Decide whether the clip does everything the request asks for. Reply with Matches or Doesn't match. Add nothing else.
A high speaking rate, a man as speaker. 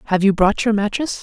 Doesn't match